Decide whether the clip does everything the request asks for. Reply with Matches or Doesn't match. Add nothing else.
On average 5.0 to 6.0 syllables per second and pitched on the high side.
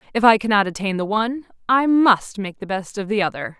Matches